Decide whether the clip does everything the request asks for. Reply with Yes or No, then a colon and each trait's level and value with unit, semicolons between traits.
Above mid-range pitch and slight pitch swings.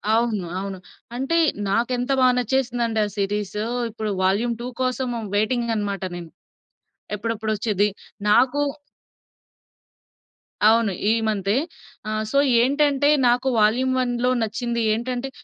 No: high, 230 Hz; average, 3.1 semitones